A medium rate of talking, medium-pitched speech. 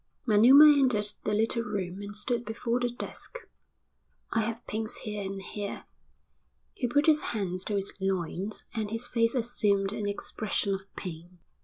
No: average, 160 wpm; high, 210 Hz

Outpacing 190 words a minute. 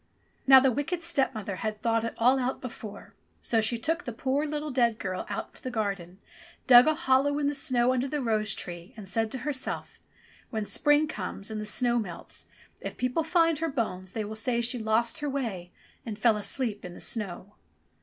Yes: fast, 205 wpm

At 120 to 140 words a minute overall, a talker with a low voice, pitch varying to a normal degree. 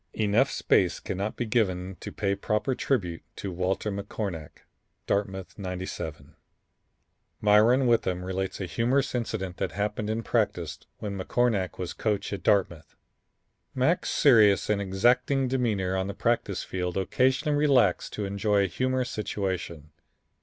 Yes: slow, 135 wpm; low, 100 Hz; average, 4.0 semitones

